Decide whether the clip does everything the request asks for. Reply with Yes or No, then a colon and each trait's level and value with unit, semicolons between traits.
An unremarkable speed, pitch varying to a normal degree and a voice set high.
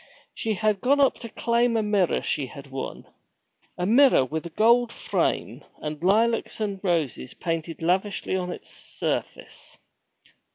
No: average, 150 wpm; wide, 5.7 semitones; high, 195 Hz